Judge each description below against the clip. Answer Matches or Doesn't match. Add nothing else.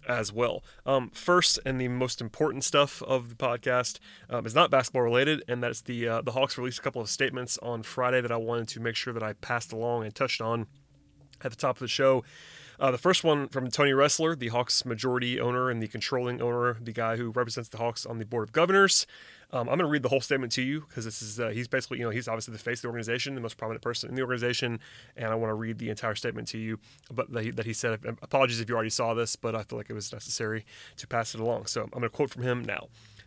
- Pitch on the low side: Matches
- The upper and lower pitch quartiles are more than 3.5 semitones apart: Doesn't match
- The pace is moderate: Doesn't match